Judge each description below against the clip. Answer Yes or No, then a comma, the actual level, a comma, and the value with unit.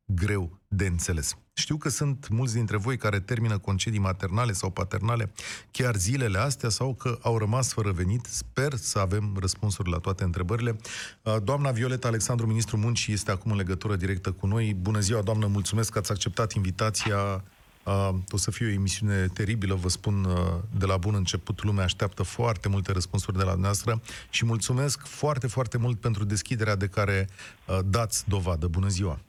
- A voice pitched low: Yes, low, 105 Hz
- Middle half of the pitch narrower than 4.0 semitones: Yes, average, 3.2 semitones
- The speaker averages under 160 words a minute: No, fast, 170 wpm